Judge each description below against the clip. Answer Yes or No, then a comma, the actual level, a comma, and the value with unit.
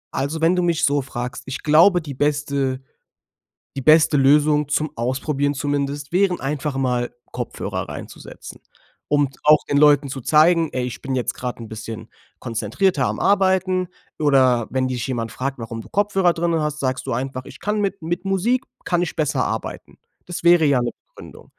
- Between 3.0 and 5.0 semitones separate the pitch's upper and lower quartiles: Yes, average, 4.5 semitones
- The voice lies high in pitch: No, medium, 145 Hz